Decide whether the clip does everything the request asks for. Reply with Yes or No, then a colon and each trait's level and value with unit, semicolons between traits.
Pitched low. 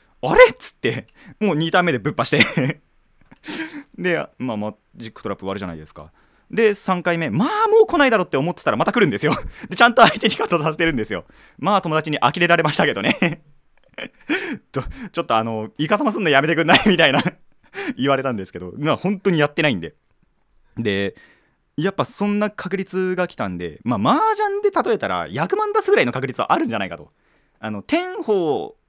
No: medium, 185 Hz